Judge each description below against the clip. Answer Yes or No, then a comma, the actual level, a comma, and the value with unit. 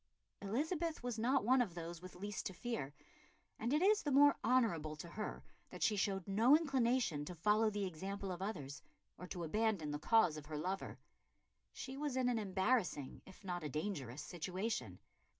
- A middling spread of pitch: No, wide, 6.4 semitones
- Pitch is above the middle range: Yes, high, 200 Hz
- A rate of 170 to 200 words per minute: Yes, average, 185 wpm